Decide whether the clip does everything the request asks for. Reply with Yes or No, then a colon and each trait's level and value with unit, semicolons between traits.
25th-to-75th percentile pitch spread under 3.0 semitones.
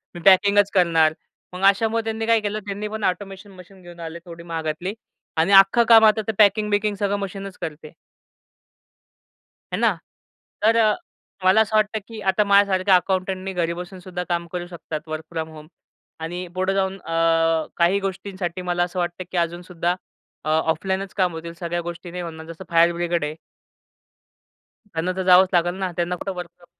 Yes: narrow, 2.6 semitones